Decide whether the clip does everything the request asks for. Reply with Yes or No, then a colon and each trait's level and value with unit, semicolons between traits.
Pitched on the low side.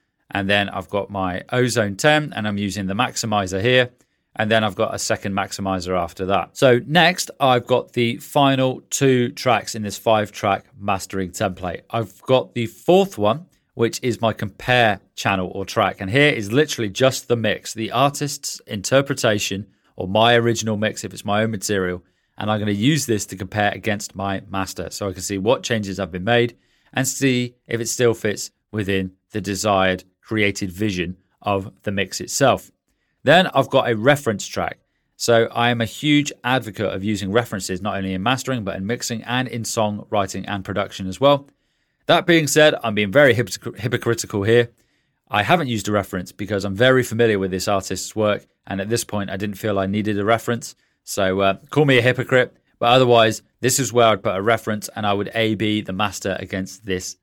Yes: low, 110 Hz